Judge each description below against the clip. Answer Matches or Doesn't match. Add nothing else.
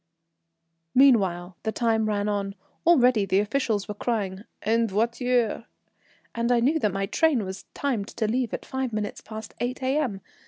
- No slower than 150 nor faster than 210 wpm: Matches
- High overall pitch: Matches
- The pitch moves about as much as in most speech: Matches